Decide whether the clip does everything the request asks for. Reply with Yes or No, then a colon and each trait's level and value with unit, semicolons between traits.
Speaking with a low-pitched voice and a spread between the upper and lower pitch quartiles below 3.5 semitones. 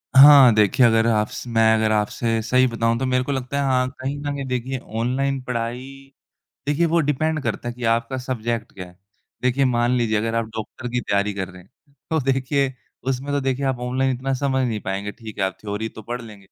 Yes: low, 125 Hz; average, 3.0 semitones